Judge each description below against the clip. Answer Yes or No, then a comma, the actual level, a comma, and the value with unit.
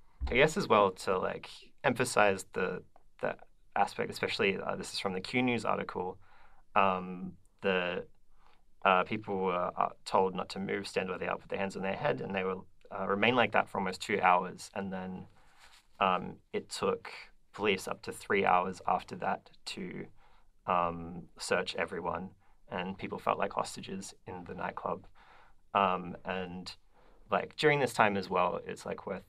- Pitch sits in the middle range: No, very low, 95 Hz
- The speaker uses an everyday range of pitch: No, narrow, 1.3 semitones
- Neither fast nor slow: Yes, average, 170 wpm